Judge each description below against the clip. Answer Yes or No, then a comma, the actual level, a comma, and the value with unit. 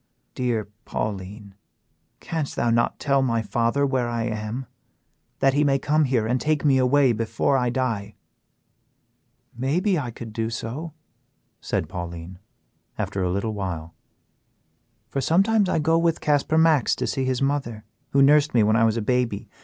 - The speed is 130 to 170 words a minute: Yes, average, 160 wpm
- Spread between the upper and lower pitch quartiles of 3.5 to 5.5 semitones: Yes, average, 4.5 semitones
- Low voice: Yes, low, 125 Hz